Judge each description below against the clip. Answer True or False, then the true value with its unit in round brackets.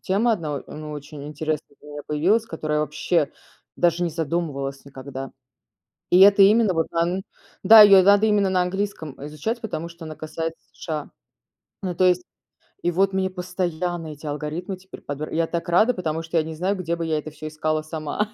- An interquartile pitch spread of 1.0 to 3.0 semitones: False (3.5 semitones)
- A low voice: False (165 Hz)